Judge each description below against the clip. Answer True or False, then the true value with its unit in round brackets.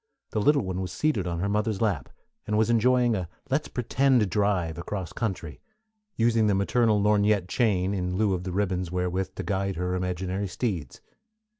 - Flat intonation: False (3.3 semitones)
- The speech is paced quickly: False (175 wpm)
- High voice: False (100 Hz)